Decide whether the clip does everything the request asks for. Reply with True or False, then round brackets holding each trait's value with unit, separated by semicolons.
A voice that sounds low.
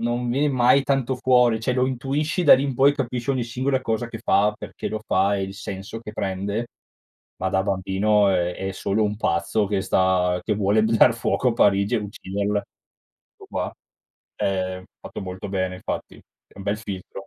True (105 Hz)